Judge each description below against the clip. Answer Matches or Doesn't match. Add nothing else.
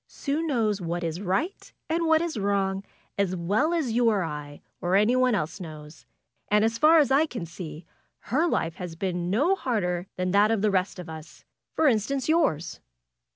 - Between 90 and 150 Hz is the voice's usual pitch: Doesn't match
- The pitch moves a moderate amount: Doesn't match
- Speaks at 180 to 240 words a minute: Matches